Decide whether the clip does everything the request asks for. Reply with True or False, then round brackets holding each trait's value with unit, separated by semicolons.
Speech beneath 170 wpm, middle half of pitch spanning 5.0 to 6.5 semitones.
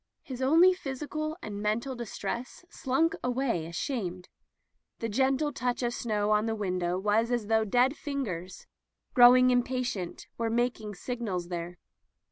False (145 wpm; 4.1 semitones)